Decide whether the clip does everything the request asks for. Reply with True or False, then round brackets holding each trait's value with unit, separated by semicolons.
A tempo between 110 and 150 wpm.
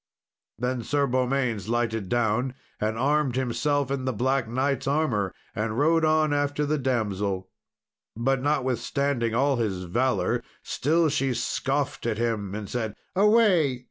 True (140 wpm)